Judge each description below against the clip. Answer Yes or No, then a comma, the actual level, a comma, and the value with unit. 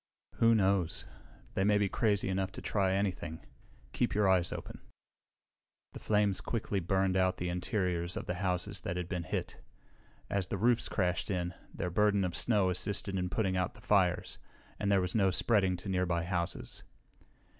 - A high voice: No, very low, 95 Hz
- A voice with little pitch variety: Yes, narrow, 2.1 semitones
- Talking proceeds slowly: No, average, 175 wpm